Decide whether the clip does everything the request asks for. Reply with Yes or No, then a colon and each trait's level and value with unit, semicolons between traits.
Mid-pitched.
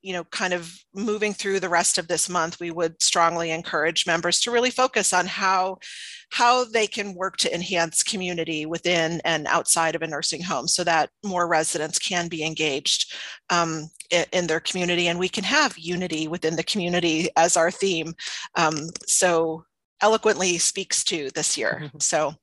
Yes: medium, 175 Hz